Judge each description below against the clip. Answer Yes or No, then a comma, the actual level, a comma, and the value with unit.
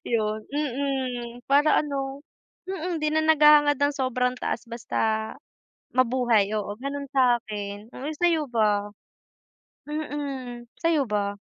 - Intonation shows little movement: No, average, 4.0 semitones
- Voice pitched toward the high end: Yes, very high, 260 Hz